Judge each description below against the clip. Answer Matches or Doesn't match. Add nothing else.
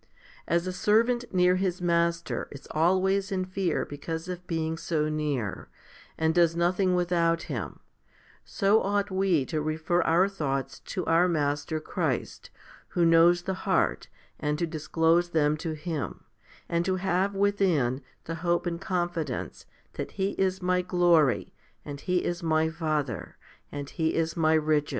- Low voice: Doesn't match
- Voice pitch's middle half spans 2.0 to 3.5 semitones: Matches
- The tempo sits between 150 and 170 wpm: Matches